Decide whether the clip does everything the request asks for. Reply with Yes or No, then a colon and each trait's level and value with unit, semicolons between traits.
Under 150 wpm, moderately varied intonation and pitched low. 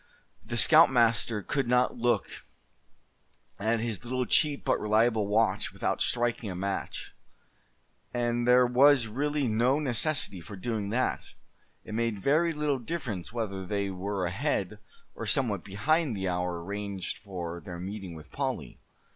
Yes: average, 140 wpm; average, 4.2 semitones; low, 115 Hz